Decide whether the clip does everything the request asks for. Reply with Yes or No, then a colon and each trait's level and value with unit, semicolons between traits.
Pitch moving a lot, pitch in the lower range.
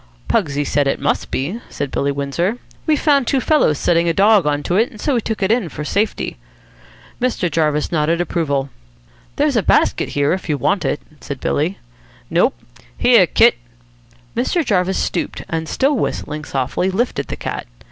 No: wide, 6.5 semitones; medium, 170 Hz